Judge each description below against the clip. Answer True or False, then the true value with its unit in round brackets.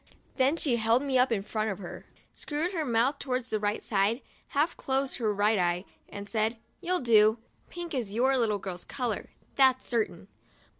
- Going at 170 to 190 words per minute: True (185 wpm)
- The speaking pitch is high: True (235 Hz)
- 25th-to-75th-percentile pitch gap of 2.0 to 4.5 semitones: True (4.2 semitones)